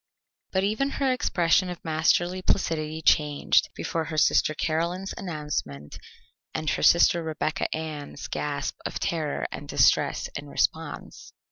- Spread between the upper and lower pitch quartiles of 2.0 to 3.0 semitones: Yes, average, 2.7 semitones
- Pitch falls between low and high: Yes, medium, 160 Hz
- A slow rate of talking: Yes, slow, 130 wpm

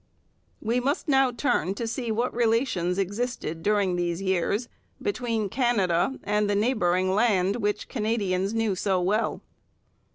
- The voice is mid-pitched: No, high, 210 Hz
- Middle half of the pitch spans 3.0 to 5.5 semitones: Yes, average, 4.2 semitones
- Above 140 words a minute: No, slow, 135 wpm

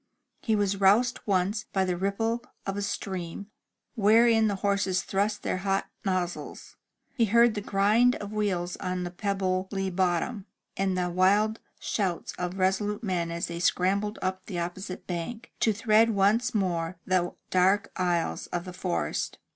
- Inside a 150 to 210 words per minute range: Yes, average, 160 wpm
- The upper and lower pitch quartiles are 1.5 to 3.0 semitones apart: Yes, narrow, 2.5 semitones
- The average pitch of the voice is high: Yes, high, 195 Hz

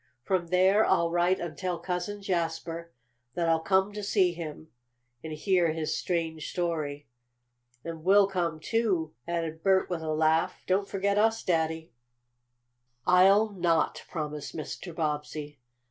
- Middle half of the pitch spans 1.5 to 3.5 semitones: Yes, average, 2.9 semitones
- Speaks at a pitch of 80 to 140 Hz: No, medium, 170 Hz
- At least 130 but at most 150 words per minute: Yes, average, 140 wpm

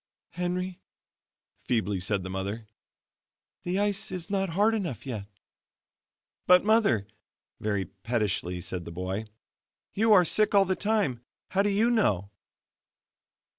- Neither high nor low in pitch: Yes, medium, 165 Hz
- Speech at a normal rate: No, slow, 130 wpm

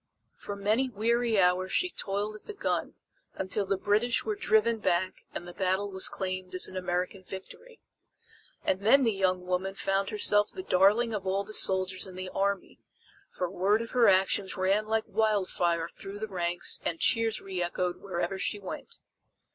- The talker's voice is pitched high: Yes, high, 195 Hz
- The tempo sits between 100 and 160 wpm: No, average, 175 wpm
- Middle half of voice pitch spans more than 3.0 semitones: No, narrow, 2.4 semitones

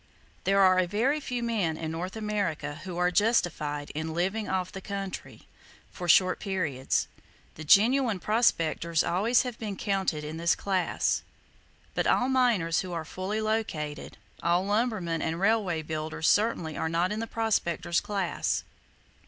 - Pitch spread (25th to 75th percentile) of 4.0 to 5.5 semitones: Yes, average, 4.6 semitones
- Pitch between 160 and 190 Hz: Yes, medium, 185 Hz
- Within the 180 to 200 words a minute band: No, average, 155 wpm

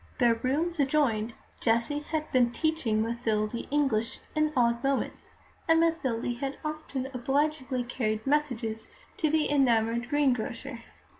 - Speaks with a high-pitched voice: Yes, very high, 255 Hz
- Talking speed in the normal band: No, slow, 125 wpm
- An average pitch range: Yes, average, 4.2 semitones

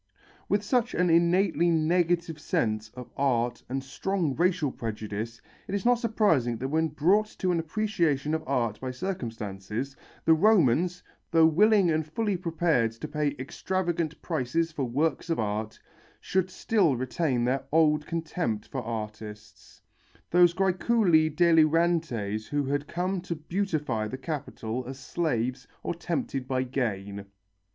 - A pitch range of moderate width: No, wide, 5.8 semitones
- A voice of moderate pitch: Yes, medium, 155 Hz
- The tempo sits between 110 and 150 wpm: Yes, average, 140 wpm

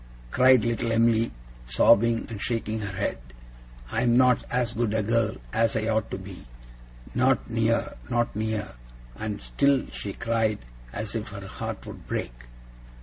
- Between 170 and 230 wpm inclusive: No, average, 155 wpm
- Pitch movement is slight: Yes, narrow, 2.0 semitones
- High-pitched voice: No, low, 110 Hz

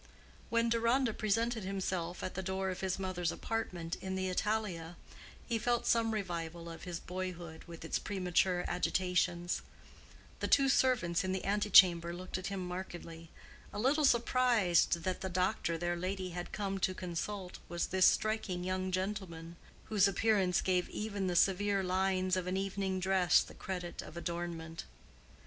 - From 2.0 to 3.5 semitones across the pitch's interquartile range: Yes, narrow, 2.4 semitones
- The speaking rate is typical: Yes, average, 160 wpm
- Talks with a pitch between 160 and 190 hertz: Yes, medium, 185 Hz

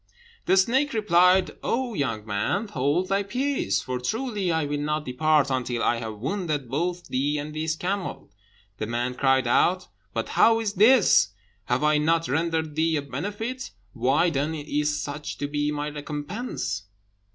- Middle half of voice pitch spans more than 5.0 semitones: Yes, wide, 5.4 semitones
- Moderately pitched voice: Yes, medium, 150 Hz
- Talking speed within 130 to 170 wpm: Yes, average, 165 wpm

